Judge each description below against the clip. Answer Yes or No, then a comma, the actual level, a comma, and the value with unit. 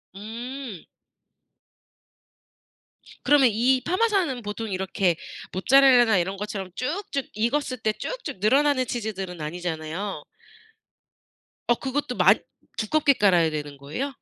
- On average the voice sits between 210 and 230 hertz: Yes, high, 225 Hz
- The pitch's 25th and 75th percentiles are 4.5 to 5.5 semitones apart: No, wide, 6.1 semitones